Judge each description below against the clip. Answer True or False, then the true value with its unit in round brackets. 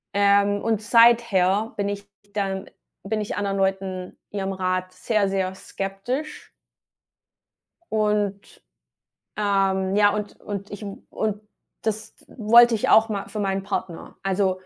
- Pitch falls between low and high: False (200 Hz)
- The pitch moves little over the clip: True (1.7 semitones)